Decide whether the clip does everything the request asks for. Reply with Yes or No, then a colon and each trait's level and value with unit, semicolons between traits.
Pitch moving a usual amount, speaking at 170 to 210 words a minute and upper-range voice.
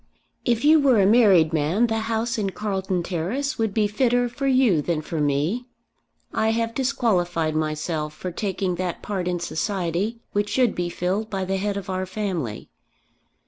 Yes: average, 4.7 semitones; average, 175 wpm; high, 195 Hz